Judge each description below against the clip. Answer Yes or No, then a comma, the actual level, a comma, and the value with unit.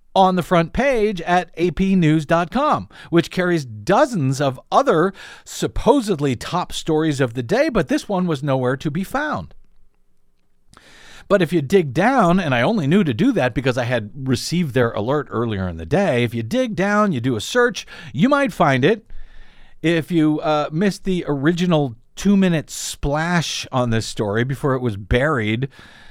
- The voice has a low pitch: No, medium, 155 Hz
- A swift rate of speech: No, average, 170 wpm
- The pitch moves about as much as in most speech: No, wide, 6.2 semitones